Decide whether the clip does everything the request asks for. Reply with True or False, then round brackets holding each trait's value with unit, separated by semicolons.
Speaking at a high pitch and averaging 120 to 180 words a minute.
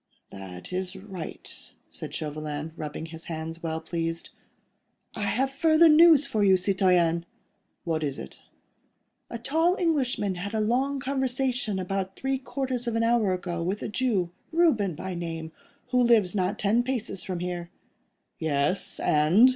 True (195 Hz; 145 wpm)